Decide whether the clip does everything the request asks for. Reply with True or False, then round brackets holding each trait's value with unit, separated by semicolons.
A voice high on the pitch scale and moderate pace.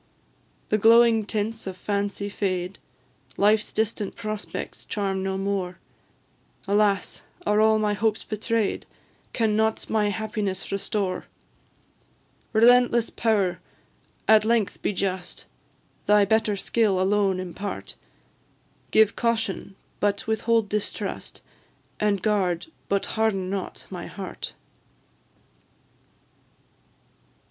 False (210 Hz; 100 wpm)